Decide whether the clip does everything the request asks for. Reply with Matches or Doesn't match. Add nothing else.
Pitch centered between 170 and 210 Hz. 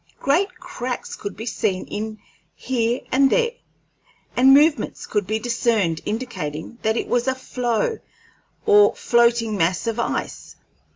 Doesn't match